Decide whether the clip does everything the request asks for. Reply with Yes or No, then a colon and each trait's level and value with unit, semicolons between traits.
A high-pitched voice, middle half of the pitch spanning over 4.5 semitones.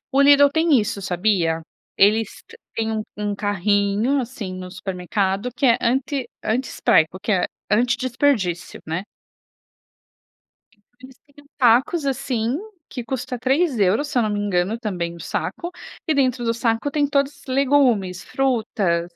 Yes: high, 230 Hz; average, 5.2 semitones